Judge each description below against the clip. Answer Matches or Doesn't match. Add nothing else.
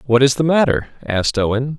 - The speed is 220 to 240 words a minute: Doesn't match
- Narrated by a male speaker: Matches